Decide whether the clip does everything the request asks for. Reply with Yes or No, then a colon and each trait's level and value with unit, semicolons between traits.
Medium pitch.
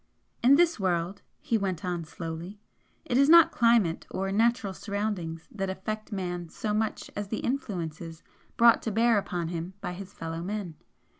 No: high, 195 Hz